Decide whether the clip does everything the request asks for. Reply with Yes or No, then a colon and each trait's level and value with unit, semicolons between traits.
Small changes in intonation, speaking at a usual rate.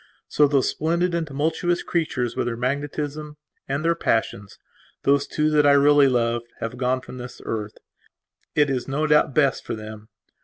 No: average, 3.7 semitones; average, 160 wpm